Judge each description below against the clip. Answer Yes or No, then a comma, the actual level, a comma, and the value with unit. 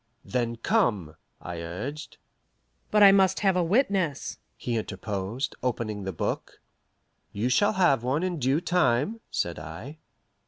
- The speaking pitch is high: No, low, 130 Hz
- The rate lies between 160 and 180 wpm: No, average, 140 wpm